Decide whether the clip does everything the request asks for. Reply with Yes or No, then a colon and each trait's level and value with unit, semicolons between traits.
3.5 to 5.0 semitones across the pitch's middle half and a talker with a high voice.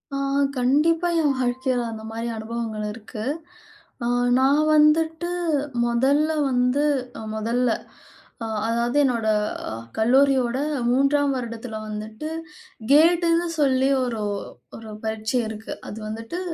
Yes: average, 4.1 semitones; very high, 250 Hz